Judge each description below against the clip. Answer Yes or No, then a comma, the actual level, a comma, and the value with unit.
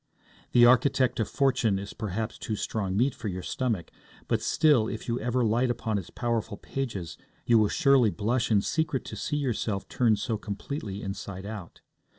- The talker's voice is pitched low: Yes, low, 115 Hz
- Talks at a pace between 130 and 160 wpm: No, average, 175 wpm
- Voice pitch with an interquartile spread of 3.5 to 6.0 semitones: Yes, average, 3.8 semitones